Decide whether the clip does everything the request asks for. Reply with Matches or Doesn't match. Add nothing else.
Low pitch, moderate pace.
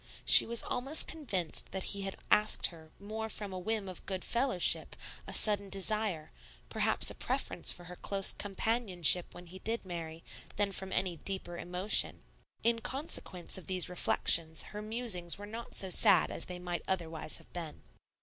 Doesn't match